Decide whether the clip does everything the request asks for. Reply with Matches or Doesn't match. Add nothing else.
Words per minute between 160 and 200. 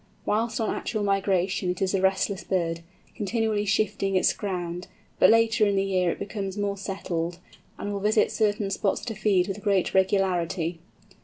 Matches